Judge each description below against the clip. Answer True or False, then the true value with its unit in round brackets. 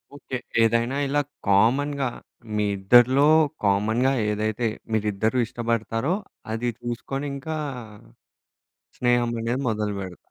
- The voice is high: False (115 Hz)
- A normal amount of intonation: True (3.4 semitones)